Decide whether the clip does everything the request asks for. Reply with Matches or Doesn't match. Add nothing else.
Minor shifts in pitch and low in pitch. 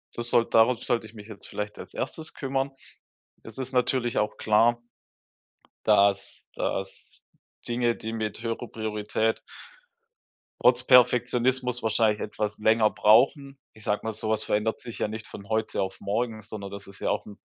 Matches